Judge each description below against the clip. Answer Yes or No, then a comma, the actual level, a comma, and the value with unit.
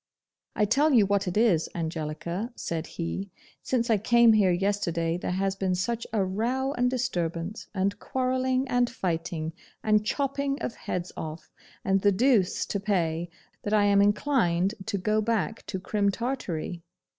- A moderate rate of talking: Yes, average, 160 wpm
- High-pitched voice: Yes, high, 200 Hz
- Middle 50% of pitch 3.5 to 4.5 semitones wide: No, average, 4.9 semitones